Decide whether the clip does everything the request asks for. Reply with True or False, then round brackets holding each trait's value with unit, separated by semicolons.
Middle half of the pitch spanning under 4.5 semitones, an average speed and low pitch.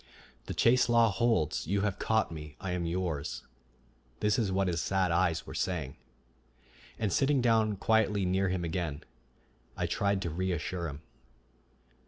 True (3.9 semitones; 155 wpm; 95 Hz)